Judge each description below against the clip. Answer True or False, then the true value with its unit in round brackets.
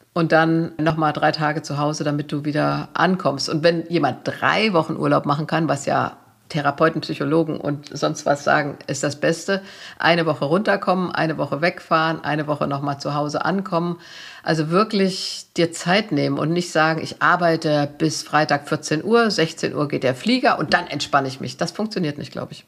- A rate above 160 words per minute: True (190 wpm)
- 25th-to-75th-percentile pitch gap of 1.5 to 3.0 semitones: True (2.6 semitones)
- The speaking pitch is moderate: True (160 Hz)